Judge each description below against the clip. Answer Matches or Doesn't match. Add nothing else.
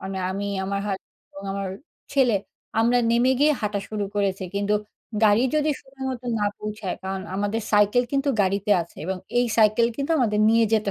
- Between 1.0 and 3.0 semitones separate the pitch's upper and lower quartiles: Doesn't match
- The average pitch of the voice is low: Doesn't match